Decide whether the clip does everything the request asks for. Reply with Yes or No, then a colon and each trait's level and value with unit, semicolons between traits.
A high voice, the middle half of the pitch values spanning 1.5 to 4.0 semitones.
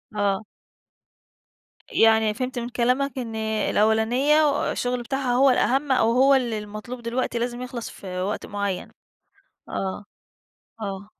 Yes: high, 235 Hz; average, 3.2 semitones